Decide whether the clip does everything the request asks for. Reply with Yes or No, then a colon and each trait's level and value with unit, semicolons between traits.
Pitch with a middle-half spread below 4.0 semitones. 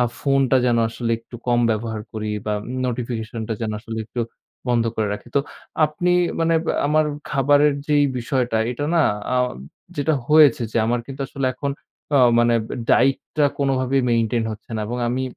Yes: average, 3.4 semitones